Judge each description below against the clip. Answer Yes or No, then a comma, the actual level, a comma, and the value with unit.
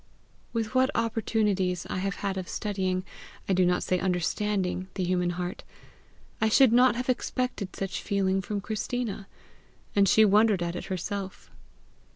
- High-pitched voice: Yes, high, 195 Hz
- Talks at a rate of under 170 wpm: Yes, average, 155 wpm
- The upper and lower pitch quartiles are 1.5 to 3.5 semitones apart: Yes, average, 3.0 semitones